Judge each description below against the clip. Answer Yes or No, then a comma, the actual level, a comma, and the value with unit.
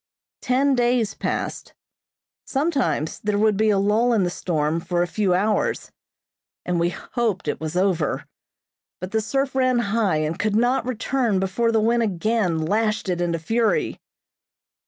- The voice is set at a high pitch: Yes, high, 215 Hz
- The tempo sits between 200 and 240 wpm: No, average, 155 wpm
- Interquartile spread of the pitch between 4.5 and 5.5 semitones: Yes, average, 4.9 semitones